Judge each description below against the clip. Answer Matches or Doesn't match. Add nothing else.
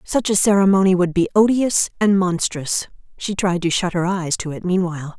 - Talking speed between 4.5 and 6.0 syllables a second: Matches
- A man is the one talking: Doesn't match